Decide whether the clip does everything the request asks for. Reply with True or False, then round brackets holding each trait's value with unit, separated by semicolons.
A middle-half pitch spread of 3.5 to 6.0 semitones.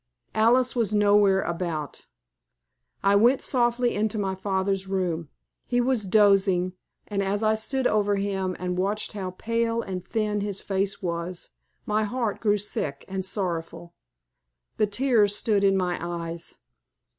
False (2.8 semitones)